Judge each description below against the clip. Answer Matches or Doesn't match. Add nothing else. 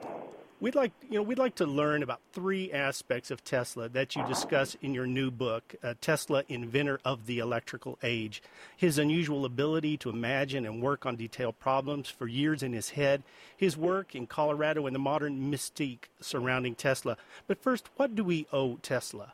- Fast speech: Doesn't match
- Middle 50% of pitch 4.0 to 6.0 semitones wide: Doesn't match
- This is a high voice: Doesn't match